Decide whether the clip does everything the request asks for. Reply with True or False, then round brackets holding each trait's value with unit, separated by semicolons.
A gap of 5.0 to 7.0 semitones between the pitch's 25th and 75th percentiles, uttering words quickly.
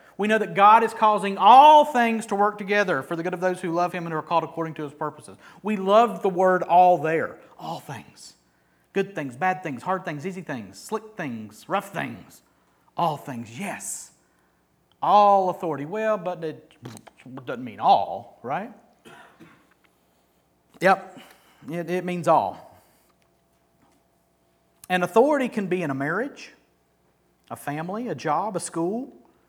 False (5.5 semitones; 155 wpm)